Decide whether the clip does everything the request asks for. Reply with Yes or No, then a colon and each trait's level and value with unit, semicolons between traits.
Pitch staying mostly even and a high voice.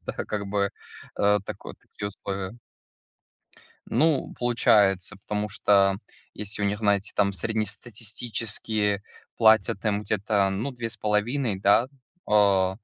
No: narrow, 1.9 semitones; low, 105 Hz